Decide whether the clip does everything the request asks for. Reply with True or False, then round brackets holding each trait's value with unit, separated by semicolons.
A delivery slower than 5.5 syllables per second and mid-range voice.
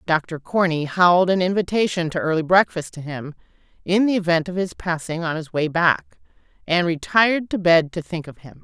True (5.2 syllables/s; 170 Hz)